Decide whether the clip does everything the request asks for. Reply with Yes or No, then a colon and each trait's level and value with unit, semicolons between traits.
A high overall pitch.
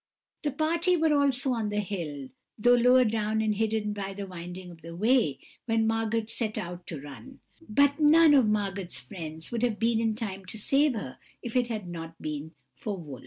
Yes: high, 215 Hz